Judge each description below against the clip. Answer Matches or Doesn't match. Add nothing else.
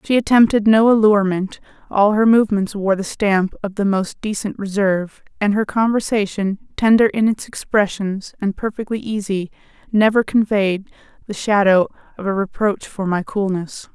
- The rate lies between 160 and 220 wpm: Doesn't match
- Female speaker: Matches